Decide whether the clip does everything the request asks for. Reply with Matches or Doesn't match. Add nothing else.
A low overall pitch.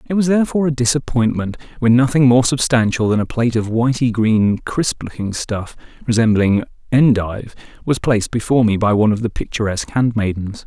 Matches